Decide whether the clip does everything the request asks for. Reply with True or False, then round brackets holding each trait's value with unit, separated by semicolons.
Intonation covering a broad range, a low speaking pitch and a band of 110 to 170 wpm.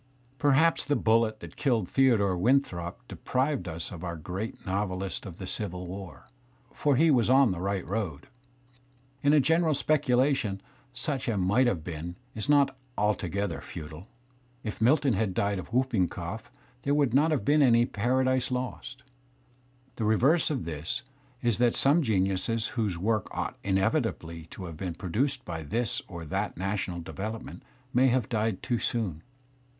True (5.9 semitones; 110 Hz; 160 wpm)